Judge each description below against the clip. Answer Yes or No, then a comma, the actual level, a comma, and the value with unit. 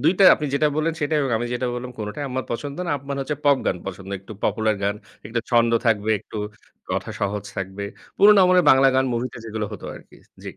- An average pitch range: Yes, average, 4.9 semitones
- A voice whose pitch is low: Yes, low, 125 Hz